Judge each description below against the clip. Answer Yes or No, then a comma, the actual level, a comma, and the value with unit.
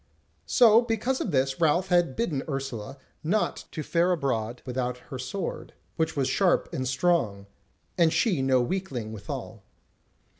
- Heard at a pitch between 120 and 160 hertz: Yes, medium, 140 Hz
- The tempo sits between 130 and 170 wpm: Yes, average, 145 wpm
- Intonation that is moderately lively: No, wide, 5.8 semitones